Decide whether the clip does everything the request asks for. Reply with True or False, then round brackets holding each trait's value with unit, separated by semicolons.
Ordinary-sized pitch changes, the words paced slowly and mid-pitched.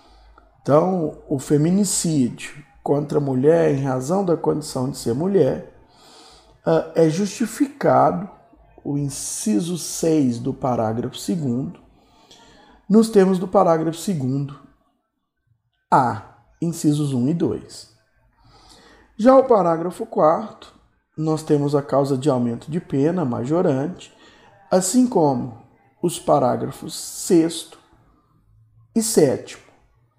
True (4.9 semitones; 100 wpm; 155 Hz)